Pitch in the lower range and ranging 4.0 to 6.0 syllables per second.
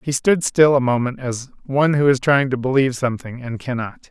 Yes: low, 130 Hz; 5.7 syllables/s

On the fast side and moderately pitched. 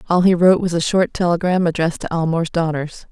Yes: fast, 210 wpm; medium, 170 Hz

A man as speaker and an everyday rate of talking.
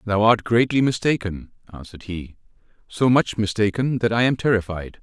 Yes: male; average, 155 wpm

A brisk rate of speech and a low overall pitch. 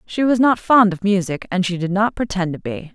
No: fast, 265 wpm; high, 195 Hz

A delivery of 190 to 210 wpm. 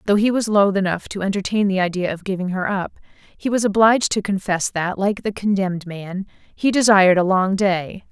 Yes: fast, 205 wpm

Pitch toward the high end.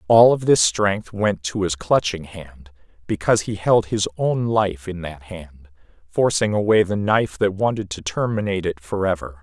No: very low, 95 Hz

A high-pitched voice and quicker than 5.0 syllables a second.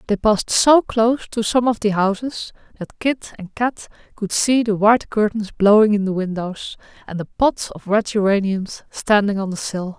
No: high, 210 Hz; 4.7 syllables/s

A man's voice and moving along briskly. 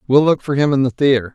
Yes: male; fast, 310 wpm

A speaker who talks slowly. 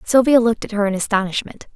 No: fast, 205 wpm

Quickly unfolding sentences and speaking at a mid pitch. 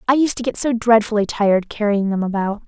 No: fast, 225 wpm; high, 220 Hz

